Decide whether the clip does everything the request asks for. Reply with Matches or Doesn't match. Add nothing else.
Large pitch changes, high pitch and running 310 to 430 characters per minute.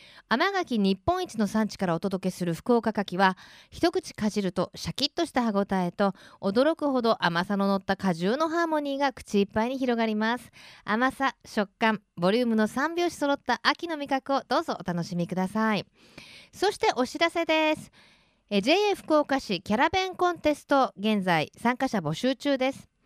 Matches